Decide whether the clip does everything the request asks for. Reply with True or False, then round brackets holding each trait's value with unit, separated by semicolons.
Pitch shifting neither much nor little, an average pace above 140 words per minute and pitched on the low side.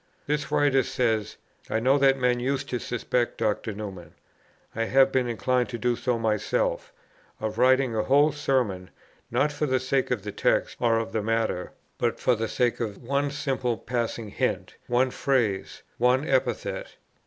True (3.0 semitones; 170 wpm; 125 Hz)